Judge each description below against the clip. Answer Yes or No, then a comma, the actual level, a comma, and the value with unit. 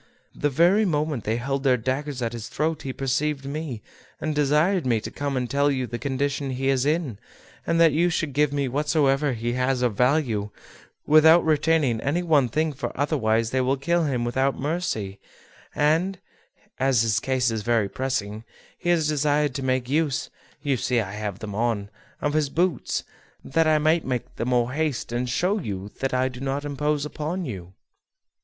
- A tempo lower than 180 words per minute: No, average, 190 wpm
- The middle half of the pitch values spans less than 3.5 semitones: No, average, 3.8 semitones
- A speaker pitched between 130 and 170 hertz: Yes, low, 135 Hz